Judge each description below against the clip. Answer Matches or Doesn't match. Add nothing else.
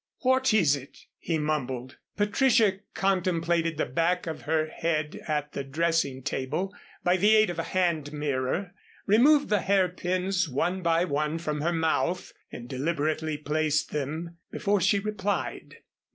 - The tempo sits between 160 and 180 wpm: Doesn't match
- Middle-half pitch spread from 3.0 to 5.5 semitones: Matches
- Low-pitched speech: Doesn't match